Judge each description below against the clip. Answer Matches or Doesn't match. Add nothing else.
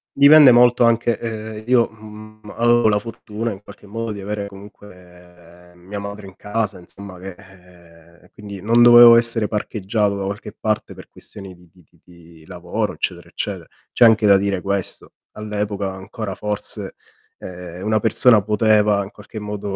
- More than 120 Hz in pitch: Doesn't match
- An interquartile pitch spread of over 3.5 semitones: Doesn't match